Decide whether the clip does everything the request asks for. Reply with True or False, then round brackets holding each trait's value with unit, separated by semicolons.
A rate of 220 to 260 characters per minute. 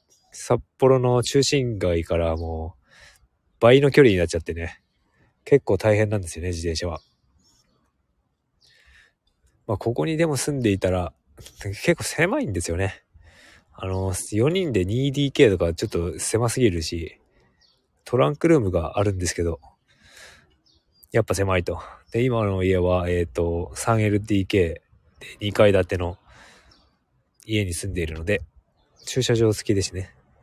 True (255 characters per minute)